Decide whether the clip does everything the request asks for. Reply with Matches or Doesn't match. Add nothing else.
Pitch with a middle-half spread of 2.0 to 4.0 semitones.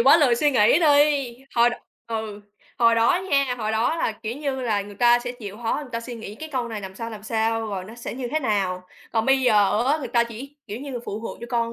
Matches